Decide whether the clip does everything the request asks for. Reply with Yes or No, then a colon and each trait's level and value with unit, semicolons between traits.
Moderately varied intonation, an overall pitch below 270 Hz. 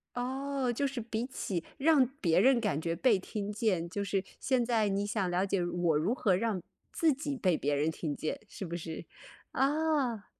No: wide, 6.6 semitones; high, 210 Hz